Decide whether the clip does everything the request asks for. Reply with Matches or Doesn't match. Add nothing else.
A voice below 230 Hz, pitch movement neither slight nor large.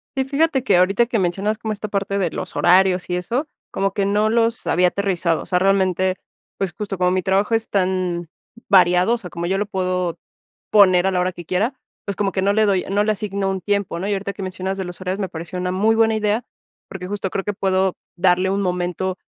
Doesn't match